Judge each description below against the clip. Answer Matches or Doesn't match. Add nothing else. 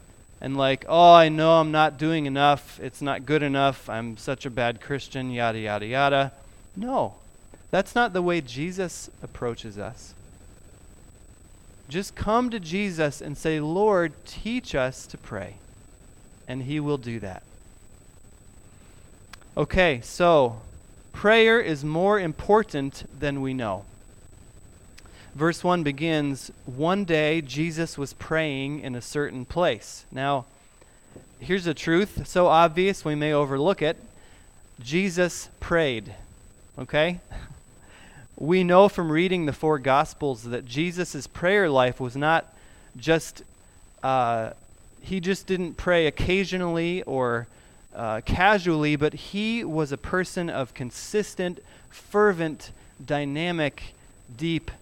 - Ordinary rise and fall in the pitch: Doesn't match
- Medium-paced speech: Doesn't match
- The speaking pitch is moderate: Matches